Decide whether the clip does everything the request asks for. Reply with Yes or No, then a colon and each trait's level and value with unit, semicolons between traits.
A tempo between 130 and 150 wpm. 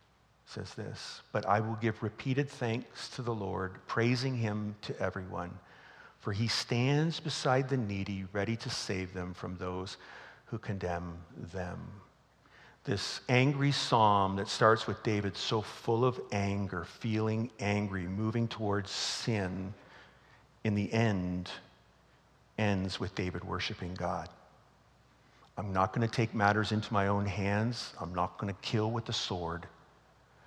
Yes: average, 140 wpm